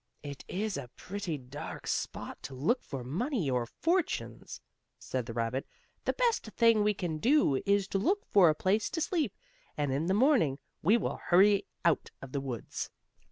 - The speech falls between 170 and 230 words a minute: Yes, average, 180 wpm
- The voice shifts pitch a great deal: Yes, wide, 8.4 semitones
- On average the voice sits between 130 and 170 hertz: No, medium, 180 Hz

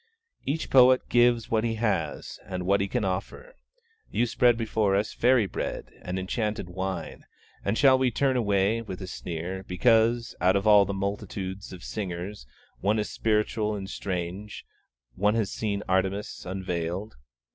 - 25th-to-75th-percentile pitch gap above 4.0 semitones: No, average, 3.2 semitones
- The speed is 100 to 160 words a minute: Yes, average, 155 wpm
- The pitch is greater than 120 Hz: No, low, 100 Hz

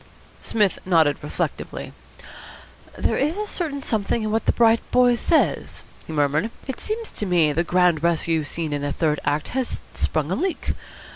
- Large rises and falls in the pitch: Yes, wide, 7.7 semitones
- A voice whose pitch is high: No, medium, 180 Hz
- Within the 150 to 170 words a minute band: Yes, average, 165 wpm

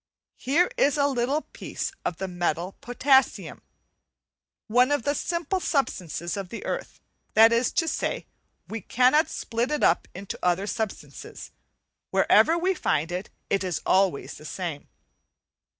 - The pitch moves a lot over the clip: Yes, wide, 8.0 semitones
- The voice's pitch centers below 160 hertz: No, high, 230 Hz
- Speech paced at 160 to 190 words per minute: No, average, 145 wpm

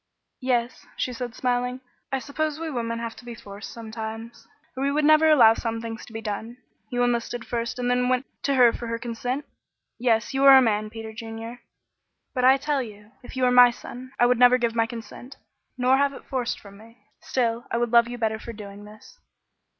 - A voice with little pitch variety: Yes, narrow, 2.0 semitones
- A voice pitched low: No, high, 240 Hz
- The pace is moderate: No, fast, 215 wpm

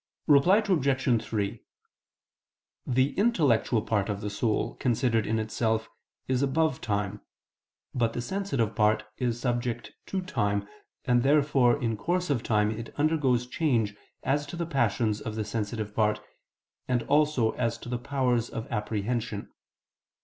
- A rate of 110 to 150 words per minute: Yes, average, 140 wpm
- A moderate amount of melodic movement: Yes, average, 4.1 semitones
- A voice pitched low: Yes, low, 120 Hz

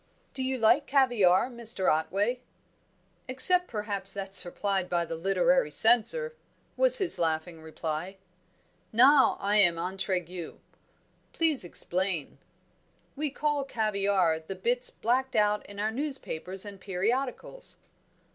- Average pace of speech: No, slow, 120 wpm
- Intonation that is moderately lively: No, wide, 6.1 semitones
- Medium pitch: No, high, 205 Hz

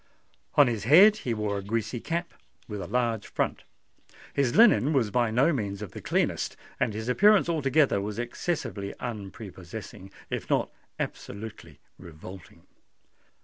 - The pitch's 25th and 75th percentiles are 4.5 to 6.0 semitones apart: Yes, wide, 5.5 semitones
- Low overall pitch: Yes, low, 115 Hz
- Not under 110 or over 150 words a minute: Yes, average, 140 wpm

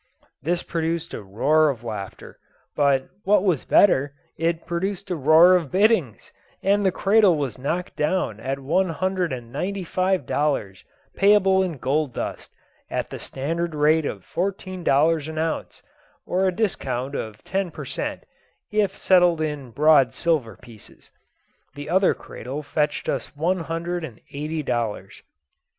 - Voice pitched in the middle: Yes, medium, 160 Hz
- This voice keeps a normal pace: Yes, average, 150 wpm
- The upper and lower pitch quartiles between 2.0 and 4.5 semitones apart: No, average, 5.0 semitones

